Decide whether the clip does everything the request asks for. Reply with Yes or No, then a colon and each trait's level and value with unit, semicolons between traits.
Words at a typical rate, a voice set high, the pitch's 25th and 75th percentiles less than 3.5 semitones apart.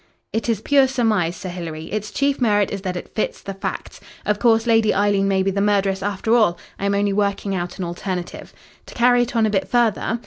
No: fast, 230 wpm; high, 205 Hz; average, 2.8 semitones